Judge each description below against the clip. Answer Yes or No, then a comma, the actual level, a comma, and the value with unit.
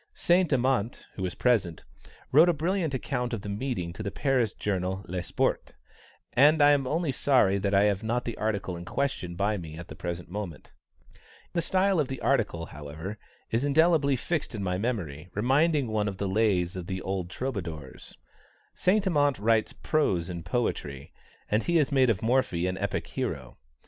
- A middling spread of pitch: No, wide, 7.1 semitones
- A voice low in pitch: Yes, low, 110 Hz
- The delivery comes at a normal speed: Yes, average, 185 wpm